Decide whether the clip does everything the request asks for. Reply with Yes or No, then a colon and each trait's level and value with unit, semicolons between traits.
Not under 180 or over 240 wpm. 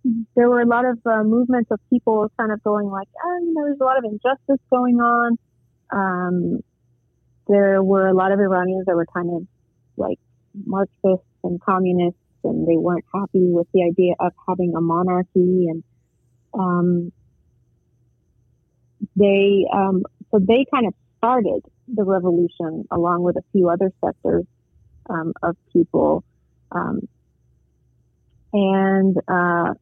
No: average, 145 wpm